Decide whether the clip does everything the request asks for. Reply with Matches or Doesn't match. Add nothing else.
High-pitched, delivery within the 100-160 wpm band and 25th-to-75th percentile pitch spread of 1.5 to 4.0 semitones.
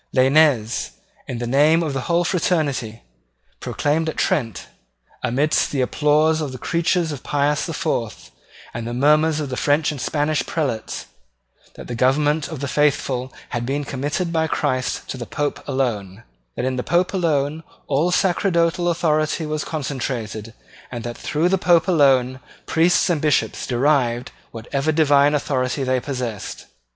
Doesn't match